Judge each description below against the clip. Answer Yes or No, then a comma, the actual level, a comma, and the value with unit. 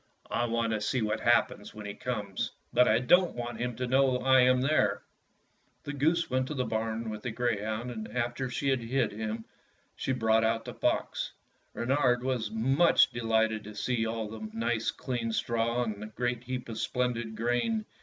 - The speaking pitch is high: No, low, 120 Hz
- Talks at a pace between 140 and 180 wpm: No, average, 195 wpm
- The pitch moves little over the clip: Yes, narrow, 2.2 semitones